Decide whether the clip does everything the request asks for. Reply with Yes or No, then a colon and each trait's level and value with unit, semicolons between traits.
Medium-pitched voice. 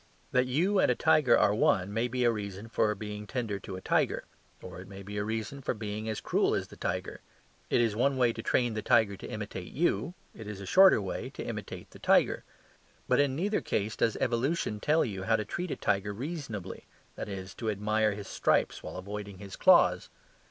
No: low, 110 Hz